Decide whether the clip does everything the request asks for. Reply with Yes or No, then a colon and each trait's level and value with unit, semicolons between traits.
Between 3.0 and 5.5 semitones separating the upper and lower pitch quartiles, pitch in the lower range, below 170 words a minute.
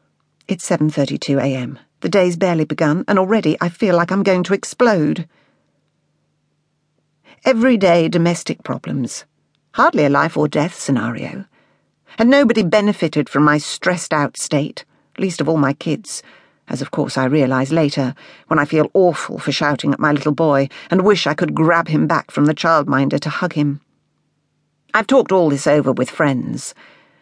No: average, 3.9 semitones; medium, 155 Hz; average, 155 wpm